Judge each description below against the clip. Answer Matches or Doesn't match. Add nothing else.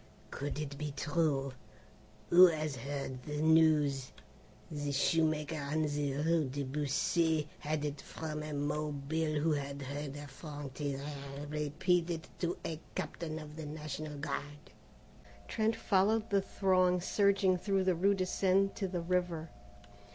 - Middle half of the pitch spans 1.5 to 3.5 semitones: Matches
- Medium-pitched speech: Matches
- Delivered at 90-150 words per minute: Matches